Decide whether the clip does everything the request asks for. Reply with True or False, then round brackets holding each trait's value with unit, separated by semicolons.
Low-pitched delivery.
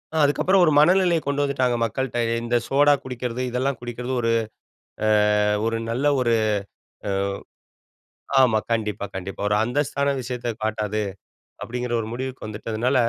True (125 Hz)